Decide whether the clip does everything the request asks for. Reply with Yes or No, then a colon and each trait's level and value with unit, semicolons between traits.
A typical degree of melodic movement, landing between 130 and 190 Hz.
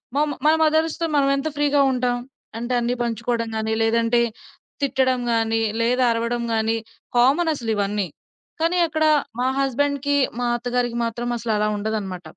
No: average, 3.6 semitones; high, 240 Hz